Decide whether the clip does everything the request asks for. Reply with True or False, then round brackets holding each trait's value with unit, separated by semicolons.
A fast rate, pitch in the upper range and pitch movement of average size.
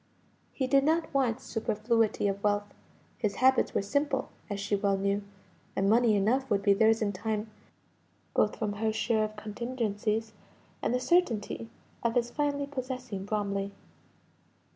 False (150 wpm; 220 Hz; 3.7 semitones)